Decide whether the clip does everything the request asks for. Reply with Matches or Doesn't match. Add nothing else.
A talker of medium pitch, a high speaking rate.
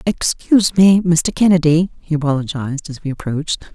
Doesn't match